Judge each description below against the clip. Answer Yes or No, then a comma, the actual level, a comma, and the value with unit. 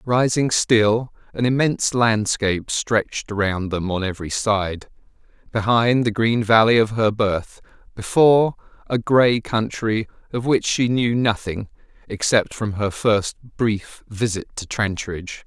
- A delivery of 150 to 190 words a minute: No, slow, 135 wpm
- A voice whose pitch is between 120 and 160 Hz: No, low, 110 Hz